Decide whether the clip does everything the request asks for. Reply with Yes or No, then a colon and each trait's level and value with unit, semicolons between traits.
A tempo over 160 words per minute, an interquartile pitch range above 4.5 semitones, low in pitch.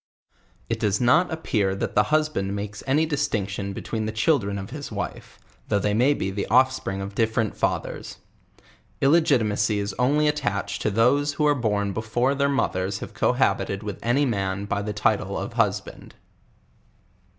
Yes: average, 175 wpm; average, 5.3 semitones; low, 110 Hz